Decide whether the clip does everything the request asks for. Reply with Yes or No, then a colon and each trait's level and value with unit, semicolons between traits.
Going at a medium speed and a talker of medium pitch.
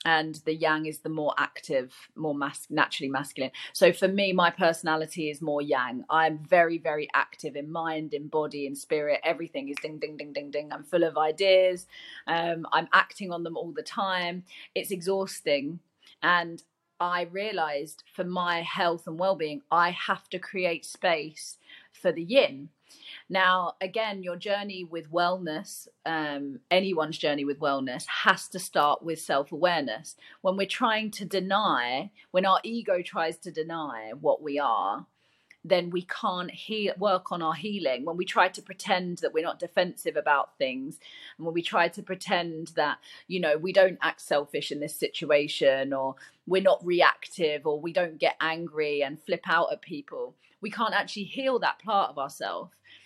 Yes: average, 175 wpm; medium, 170 Hz